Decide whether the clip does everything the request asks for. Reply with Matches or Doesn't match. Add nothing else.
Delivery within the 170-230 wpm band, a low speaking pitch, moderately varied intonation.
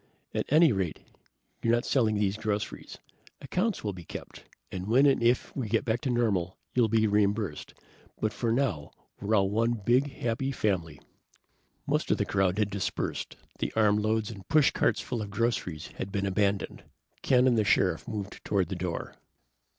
Matches